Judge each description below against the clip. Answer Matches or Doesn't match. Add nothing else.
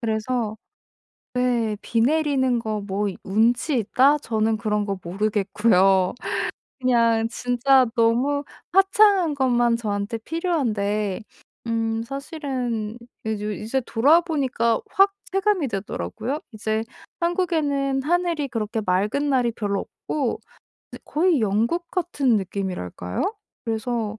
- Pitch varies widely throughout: Doesn't match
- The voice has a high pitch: Matches